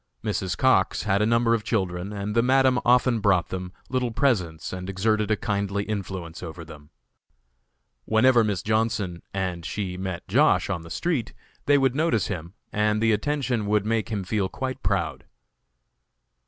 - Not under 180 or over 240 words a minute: No, average, 165 wpm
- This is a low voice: Yes, low, 105 Hz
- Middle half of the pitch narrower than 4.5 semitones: Yes, average, 3.9 semitones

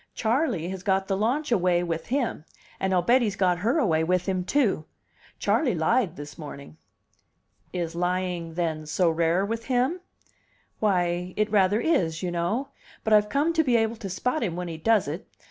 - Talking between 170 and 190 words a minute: Yes, average, 185 wpm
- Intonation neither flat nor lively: Yes, average, 4.9 semitones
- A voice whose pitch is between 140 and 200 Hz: Yes, high, 190 Hz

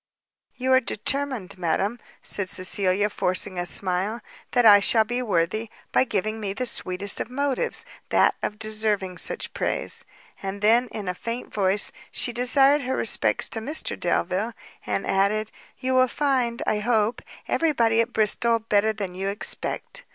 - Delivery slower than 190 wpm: Yes, average, 160 wpm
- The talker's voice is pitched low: No, high, 215 Hz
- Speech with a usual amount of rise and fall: Yes, average, 3.8 semitones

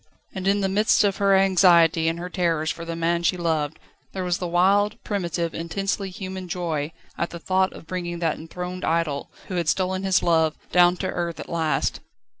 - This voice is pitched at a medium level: Yes, medium, 175 Hz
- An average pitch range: No, narrow, 2.2 semitones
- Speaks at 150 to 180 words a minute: No, average, 200 wpm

